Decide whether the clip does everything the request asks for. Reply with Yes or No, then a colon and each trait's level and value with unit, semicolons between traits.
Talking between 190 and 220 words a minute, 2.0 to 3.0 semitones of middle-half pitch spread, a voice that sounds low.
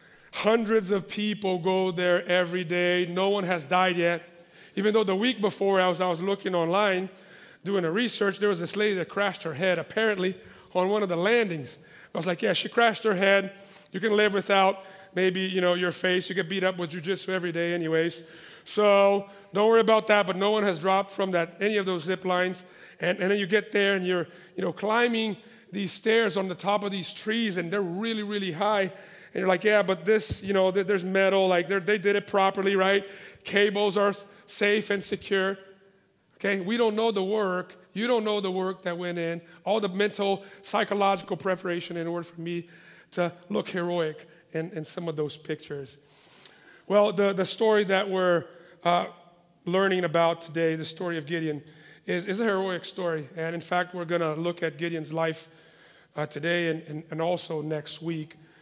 No: average, 200 wpm; average, 2.7 semitones; high, 190 Hz